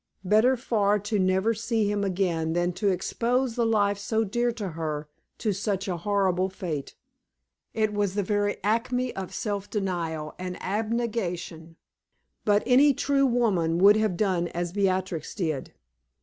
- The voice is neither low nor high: No, high, 200 Hz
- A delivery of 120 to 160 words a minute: Yes, average, 150 wpm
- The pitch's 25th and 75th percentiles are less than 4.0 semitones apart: Yes, average, 3.5 semitones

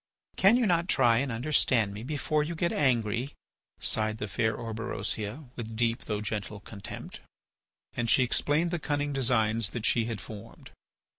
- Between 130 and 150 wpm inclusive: No, average, 160 wpm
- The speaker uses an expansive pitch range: No, average, 5.0 semitones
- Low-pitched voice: Yes, low, 115 Hz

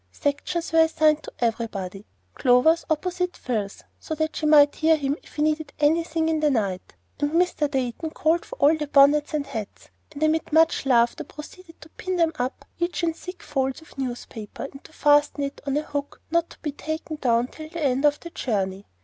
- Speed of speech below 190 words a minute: No, average, 195 wpm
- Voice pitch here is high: Yes, very high, 300 Hz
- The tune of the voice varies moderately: Yes, average, 3.3 semitones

